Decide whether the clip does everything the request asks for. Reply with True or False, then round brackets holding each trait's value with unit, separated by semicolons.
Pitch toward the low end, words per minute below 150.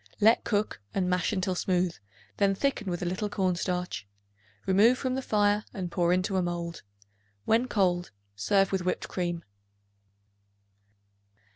False (185 Hz; 140 wpm)